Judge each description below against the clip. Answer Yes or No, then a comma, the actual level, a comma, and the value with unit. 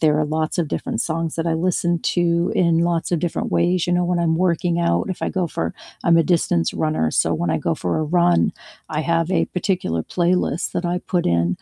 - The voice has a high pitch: No, medium, 170 Hz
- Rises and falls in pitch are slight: Yes, narrow, 2.1 semitones